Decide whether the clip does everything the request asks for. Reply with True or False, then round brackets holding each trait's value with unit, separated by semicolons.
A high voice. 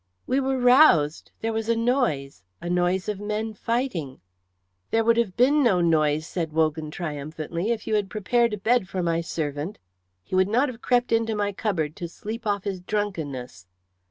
True (200 Hz)